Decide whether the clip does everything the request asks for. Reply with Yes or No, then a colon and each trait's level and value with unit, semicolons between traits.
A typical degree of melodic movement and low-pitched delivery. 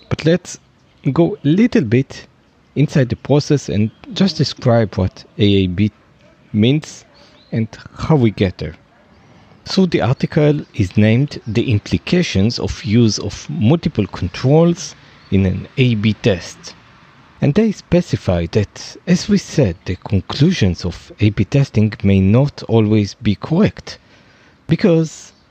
No: wide, 6.9 semitones; low, 125 Hz